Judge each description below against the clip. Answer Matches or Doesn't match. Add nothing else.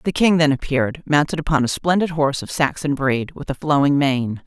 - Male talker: Doesn't match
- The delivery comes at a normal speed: Doesn't match